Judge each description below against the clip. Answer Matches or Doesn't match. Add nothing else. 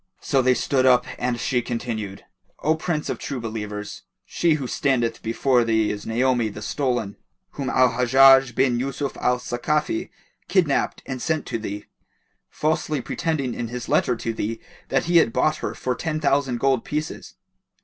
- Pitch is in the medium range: Doesn't match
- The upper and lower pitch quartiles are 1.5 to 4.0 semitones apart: Matches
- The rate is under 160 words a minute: Doesn't match